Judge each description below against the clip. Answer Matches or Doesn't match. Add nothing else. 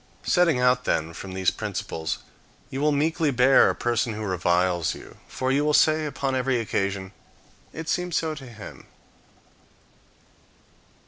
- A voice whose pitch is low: Matches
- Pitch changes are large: Matches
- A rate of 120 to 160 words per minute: Matches